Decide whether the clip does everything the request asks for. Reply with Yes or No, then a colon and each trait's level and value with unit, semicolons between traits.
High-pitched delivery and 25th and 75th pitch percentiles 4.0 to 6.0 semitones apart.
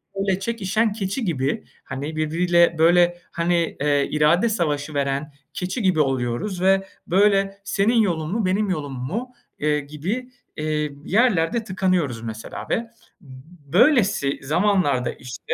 No: medium, 175 Hz; average, 5.0 semitones